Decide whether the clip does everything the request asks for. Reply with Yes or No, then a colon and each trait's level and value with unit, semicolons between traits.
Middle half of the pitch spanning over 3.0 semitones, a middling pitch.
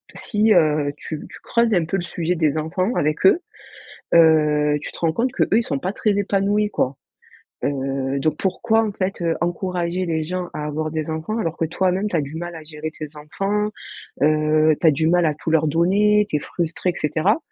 Yes: average, 3.9 semitones; medium, 165 Hz